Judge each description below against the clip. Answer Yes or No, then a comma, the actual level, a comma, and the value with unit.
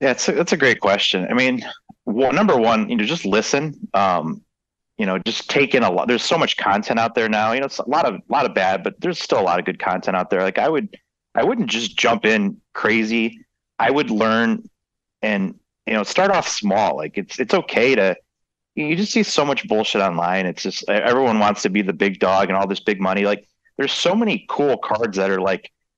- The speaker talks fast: Yes, fast, 240 wpm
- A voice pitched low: Yes, low, 110 Hz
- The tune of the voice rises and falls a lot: Yes, wide, 8.1 semitones